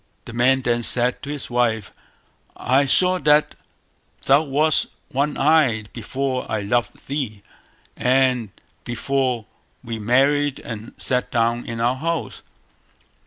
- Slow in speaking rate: Yes, slow, 125 wpm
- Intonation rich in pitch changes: No, average, 3.0 semitones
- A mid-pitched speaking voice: No, low, 125 Hz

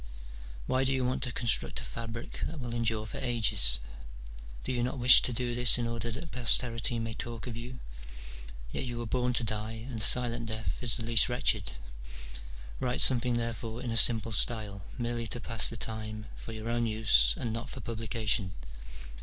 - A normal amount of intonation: No, narrow, 1.7 semitones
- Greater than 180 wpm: Yes, average, 195 wpm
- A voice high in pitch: No, low, 115 Hz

